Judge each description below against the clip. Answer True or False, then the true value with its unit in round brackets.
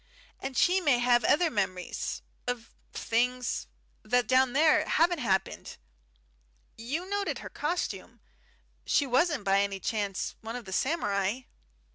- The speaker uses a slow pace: True (130 wpm)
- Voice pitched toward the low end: False (245 Hz)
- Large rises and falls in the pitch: True (6.1 semitones)